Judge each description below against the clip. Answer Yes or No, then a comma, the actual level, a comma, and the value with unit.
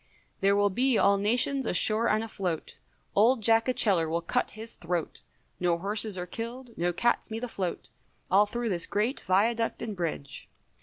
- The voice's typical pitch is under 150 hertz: No, high, 210 Hz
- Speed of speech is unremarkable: Yes, average, 165 wpm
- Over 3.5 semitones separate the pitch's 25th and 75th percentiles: Yes, average, 4.2 semitones